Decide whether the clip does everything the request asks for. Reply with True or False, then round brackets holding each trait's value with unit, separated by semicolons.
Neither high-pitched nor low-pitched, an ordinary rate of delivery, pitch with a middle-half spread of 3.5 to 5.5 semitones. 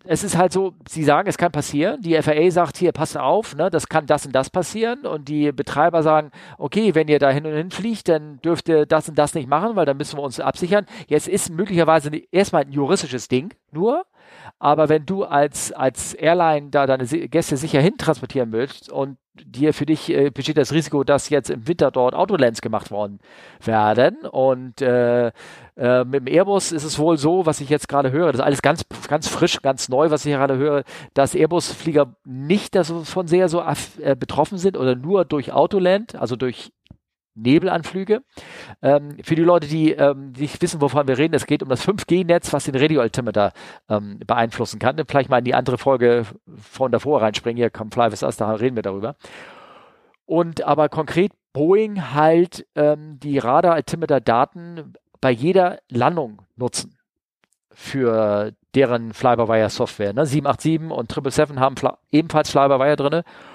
True (150 Hz; 180 wpm; 4.1 semitones)